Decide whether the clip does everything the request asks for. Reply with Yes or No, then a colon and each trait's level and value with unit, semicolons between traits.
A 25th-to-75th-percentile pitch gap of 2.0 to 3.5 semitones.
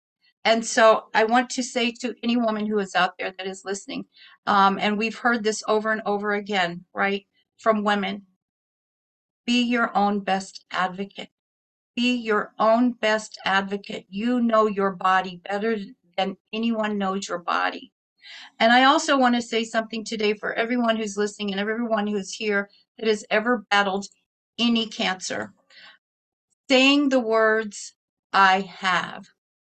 Yes: average, 2.7 semitones